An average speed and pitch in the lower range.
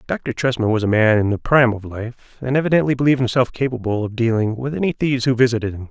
No: fast, 235 wpm; low, 120 Hz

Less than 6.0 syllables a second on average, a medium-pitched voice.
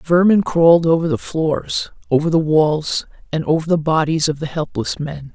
Yes: 4.7 syllables/s; medium, 160 Hz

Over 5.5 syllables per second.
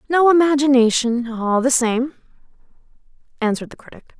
Yes: 5.7 syllables/s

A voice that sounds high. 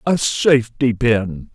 No: low, 120 Hz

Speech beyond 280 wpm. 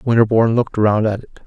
No: fast, 205 wpm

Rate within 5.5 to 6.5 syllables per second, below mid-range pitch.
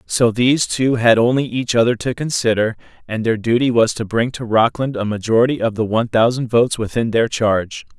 Yes: 5.6 syllables/s; low, 115 Hz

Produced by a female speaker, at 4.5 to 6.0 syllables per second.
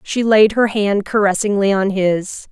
Yes: female; 4.6 syllables/s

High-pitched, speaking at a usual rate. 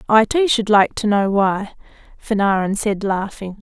Yes: high, 210 Hz; average, 165 wpm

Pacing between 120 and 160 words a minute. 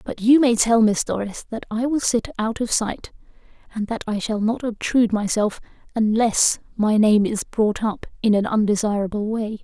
No: average, 185 wpm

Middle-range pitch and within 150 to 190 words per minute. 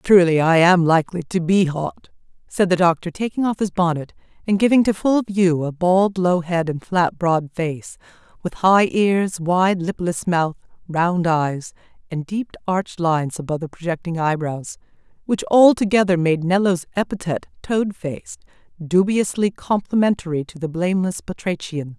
Yes: medium, 175 Hz; average, 155 wpm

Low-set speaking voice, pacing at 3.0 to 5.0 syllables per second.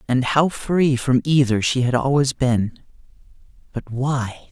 Yes: low, 130 Hz; 4.0 syllables/s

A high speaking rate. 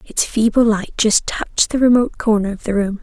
Yes: fast, 220 wpm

